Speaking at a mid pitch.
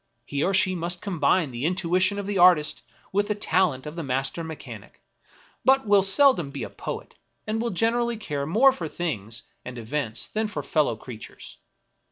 Yes: medium, 175 Hz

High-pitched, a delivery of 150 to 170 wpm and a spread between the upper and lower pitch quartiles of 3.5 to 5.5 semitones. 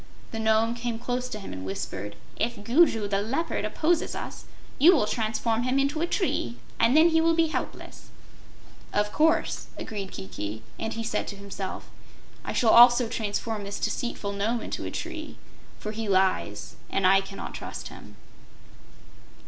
Yes: high, 225 Hz; average, 165 wpm; average, 4.2 semitones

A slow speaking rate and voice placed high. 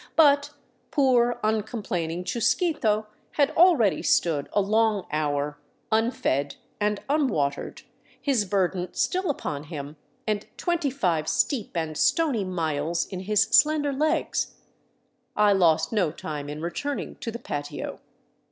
Yes: slow, 125 wpm; high, 210 Hz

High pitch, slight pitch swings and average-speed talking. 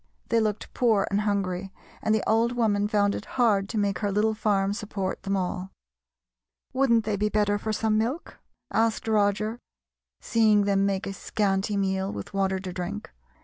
Yes: high, 205 Hz; narrow, 1.8 semitones; average, 175 wpm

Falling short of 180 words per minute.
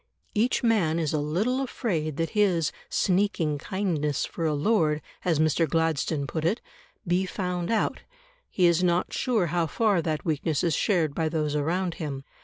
Yes: average, 170 wpm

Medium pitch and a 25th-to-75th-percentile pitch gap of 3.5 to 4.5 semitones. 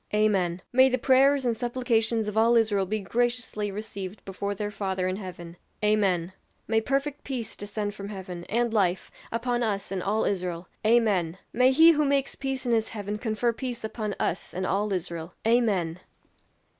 No: high, 215 Hz; average, 3.9 semitones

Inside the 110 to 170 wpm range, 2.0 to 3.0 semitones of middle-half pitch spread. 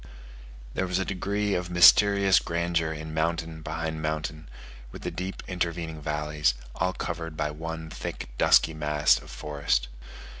Yes: average, 145 wpm; narrow, 2.5 semitones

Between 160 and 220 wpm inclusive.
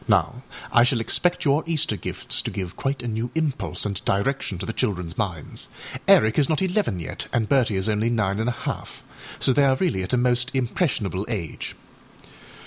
Yes: average, 195 wpm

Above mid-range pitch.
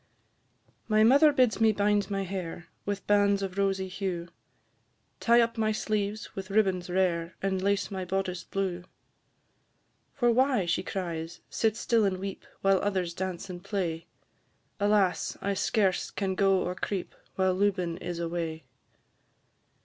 Yes: high, 195 Hz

